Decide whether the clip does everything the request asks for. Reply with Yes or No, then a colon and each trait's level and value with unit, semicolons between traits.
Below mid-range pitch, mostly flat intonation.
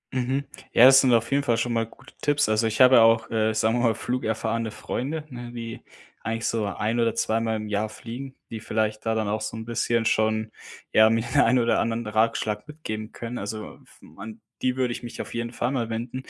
Yes: low, 115 Hz; narrow, 1.9 semitones